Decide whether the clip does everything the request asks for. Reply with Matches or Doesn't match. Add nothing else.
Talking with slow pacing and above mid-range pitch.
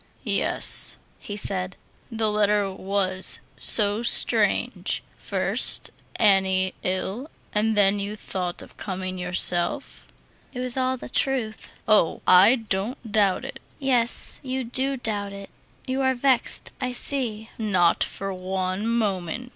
Matches